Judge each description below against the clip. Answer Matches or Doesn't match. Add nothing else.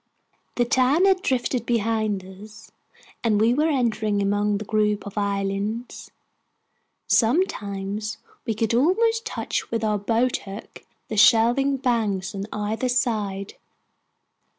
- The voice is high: Matches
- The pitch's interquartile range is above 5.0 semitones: Doesn't match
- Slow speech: Matches